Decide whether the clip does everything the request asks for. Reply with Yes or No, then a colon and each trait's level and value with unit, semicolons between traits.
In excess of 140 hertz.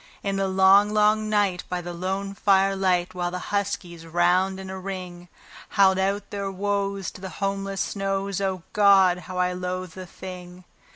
Yes: high, 190 Hz